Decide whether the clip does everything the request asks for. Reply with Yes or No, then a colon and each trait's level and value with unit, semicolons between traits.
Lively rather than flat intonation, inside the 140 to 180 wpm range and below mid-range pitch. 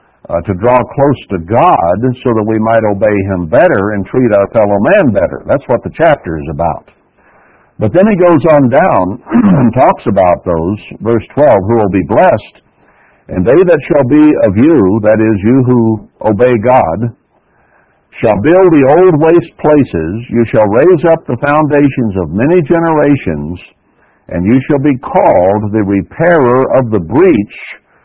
Yes: wide, 5.8 semitones; average, 170 wpm; low, 120 Hz